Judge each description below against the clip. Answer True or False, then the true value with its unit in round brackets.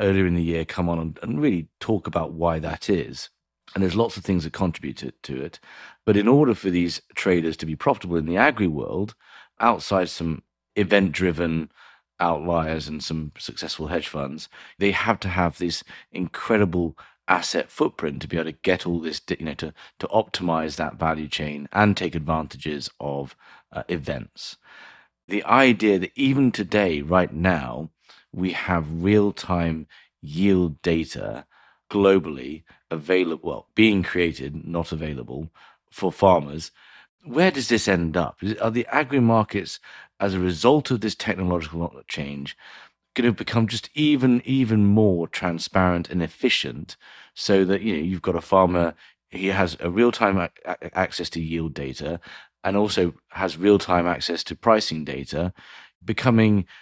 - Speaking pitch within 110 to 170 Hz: False (90 Hz)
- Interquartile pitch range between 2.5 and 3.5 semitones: False (3.9 semitones)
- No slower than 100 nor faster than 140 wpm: False (160 wpm)